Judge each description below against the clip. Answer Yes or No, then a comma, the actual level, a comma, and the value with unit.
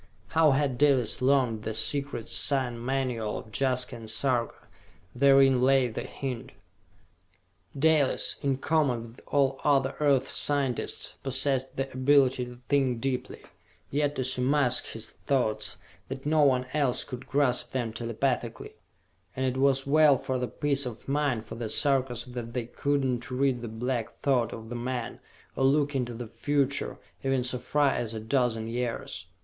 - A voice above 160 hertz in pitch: No, low, 130 Hz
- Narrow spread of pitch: Yes, narrow, 2.3 semitones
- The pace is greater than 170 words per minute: No, average, 160 wpm